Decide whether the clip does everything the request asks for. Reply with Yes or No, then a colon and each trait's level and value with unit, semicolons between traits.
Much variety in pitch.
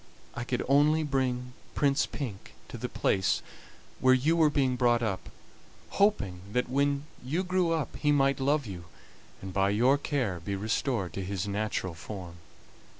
Yes: wide, 6.1 semitones